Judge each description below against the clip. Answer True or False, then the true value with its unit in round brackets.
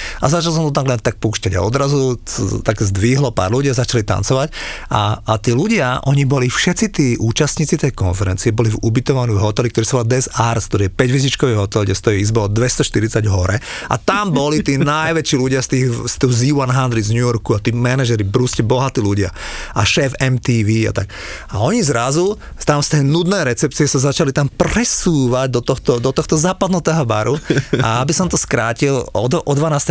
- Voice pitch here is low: True (130 Hz)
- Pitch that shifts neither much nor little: True (4.2 semitones)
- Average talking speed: False (200 wpm)